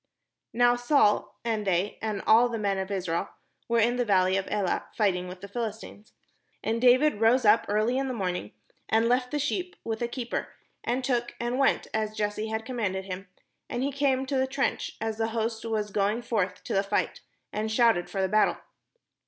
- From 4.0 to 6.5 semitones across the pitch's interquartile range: No, average, 3.2 semitones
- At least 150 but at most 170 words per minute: No, average, 200 wpm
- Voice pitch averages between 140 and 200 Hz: No, high, 220 Hz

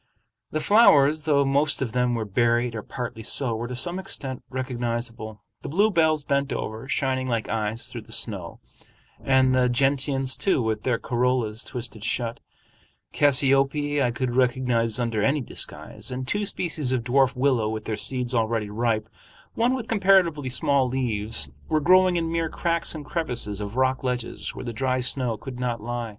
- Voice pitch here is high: No, low, 130 Hz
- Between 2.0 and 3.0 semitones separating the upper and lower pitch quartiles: No, average, 3.4 semitones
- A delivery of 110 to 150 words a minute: No, average, 170 wpm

